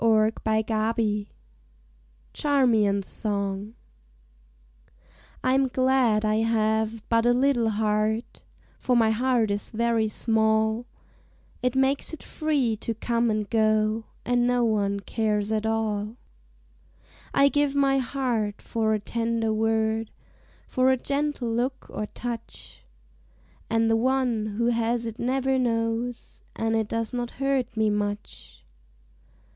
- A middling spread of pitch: No, narrow, 2.3 semitones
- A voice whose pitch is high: Yes, high, 225 Hz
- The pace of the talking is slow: Yes, slow, 125 wpm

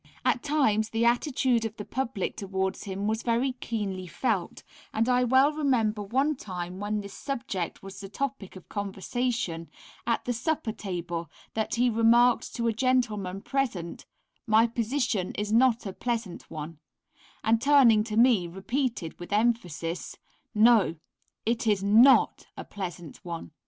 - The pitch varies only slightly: No, average, 4.1 semitones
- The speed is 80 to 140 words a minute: No, average, 150 wpm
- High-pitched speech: Yes, high, 220 Hz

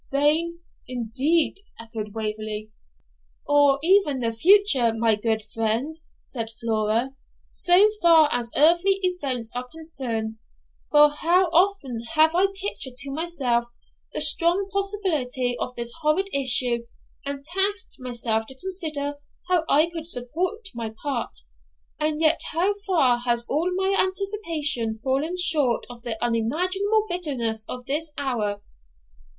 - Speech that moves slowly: Yes, slow, 130 wpm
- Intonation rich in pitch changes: Yes, wide, 6.5 semitones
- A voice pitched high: Yes, very high, 280 Hz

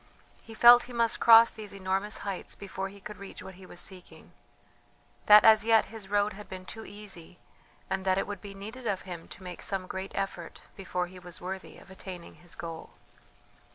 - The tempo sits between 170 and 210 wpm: Yes, average, 200 wpm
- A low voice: No, high, 195 Hz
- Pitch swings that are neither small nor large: No, narrow, 2.3 semitones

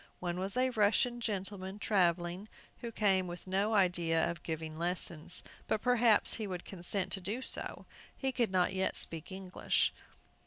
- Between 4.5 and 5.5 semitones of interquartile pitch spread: No, average, 3.4 semitones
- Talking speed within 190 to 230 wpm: No, average, 160 wpm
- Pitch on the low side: No, high, 190 Hz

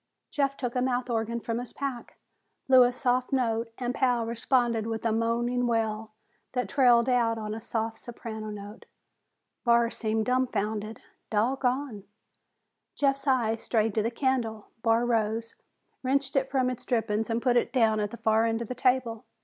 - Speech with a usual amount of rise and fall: No, narrow, 2.1 semitones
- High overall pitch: Yes, high, 235 Hz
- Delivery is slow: No, average, 170 wpm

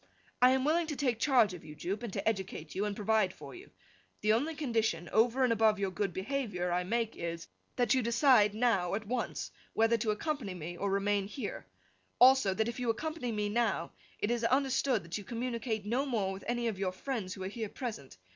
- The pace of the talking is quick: Yes, fast, 215 wpm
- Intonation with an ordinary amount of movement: Yes, average, 4.1 semitones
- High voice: Yes, high, 220 Hz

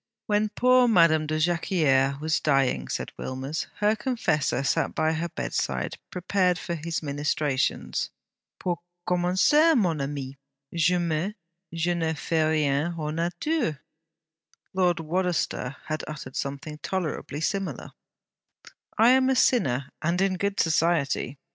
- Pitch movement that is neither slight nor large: Yes, average, 4.1 semitones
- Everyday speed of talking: No, slow, 125 wpm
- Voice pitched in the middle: Yes, medium, 165 Hz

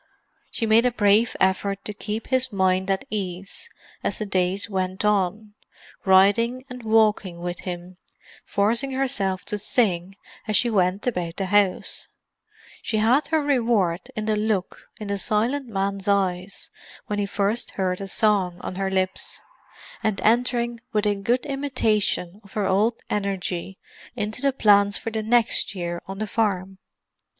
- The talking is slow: No, average, 155 wpm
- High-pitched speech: Yes, high, 205 Hz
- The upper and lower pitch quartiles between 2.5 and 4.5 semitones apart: Yes, average, 3.0 semitones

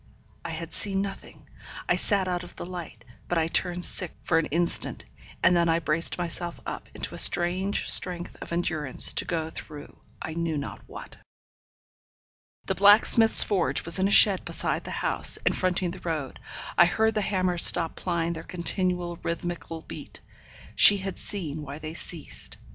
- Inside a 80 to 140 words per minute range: No, average, 175 wpm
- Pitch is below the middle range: No, medium, 175 Hz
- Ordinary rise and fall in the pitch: No, narrow, 2.1 semitones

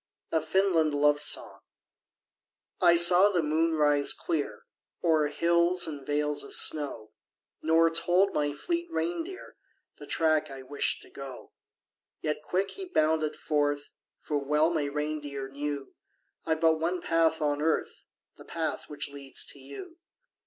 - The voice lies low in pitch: No, medium, 155 Hz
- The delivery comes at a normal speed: Yes, average, 145 wpm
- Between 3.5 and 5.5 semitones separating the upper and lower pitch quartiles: No, narrow, 2.6 semitones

